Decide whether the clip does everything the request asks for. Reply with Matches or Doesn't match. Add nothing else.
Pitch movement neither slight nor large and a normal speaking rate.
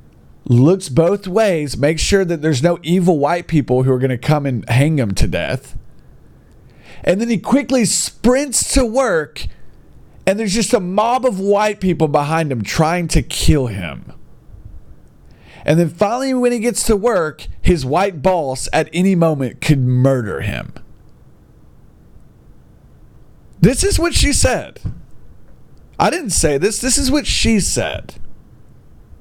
Doesn't match